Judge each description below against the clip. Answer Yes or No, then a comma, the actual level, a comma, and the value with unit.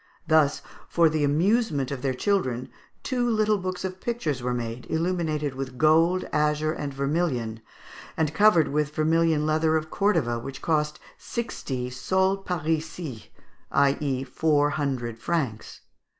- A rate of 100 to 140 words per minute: Yes, slow, 135 wpm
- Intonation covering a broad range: No, average, 4.0 semitones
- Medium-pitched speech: Yes, medium, 155 Hz